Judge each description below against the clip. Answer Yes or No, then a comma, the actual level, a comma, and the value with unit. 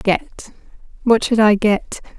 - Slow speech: Yes, slow, 110 wpm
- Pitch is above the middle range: Yes, high, 220 Hz